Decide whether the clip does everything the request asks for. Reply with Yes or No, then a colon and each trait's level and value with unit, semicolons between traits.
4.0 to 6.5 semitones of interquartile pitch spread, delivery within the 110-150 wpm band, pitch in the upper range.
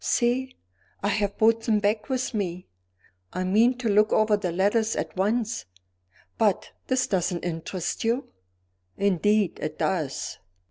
No: average, 3.4 semitones; average, 140 wpm; high, 210 Hz